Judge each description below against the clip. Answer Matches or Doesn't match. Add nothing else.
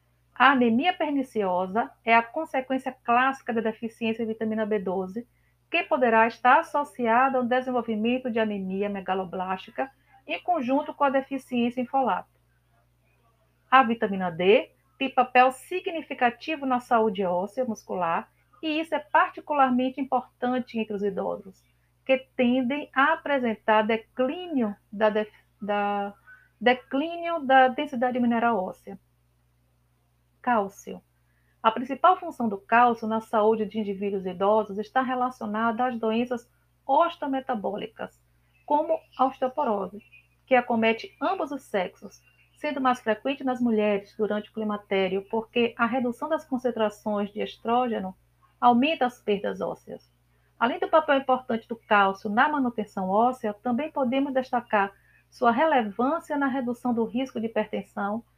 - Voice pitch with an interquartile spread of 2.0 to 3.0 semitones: Doesn't match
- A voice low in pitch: Doesn't match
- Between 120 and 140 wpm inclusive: Matches